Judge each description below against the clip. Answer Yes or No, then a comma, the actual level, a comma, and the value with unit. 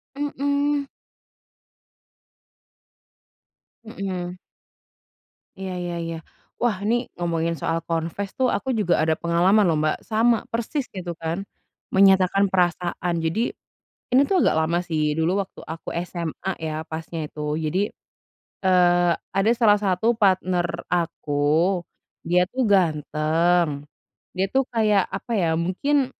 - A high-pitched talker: No, medium, 180 Hz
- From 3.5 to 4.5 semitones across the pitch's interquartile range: Yes, average, 4.0 semitones